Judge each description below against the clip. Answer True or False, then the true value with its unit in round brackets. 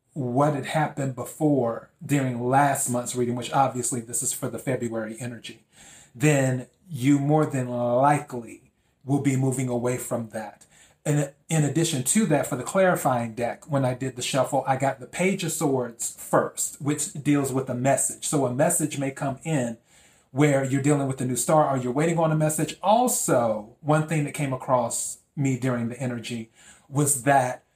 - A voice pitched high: False (135 Hz)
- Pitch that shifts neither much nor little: True (3.2 semitones)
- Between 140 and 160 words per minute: False (180 wpm)